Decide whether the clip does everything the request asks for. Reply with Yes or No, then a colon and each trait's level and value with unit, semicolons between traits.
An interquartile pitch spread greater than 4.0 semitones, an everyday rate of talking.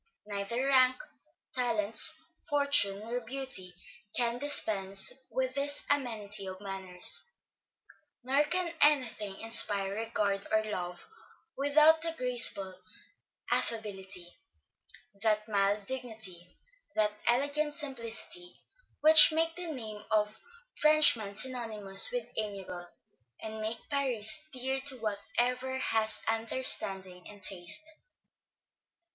No: average, 5.1 semitones; slow, 105 wpm